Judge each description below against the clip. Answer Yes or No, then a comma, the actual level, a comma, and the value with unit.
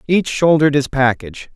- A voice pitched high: No, medium, 140 Hz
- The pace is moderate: Yes, average, 155 wpm